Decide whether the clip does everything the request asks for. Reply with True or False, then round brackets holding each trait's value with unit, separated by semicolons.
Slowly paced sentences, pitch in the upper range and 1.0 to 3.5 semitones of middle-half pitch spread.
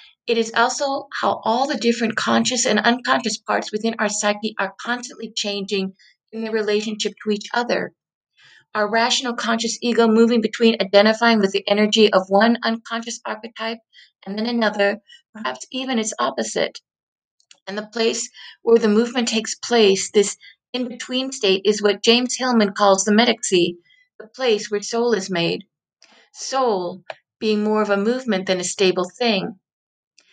False (155 wpm; 220 Hz; 2.4 semitones)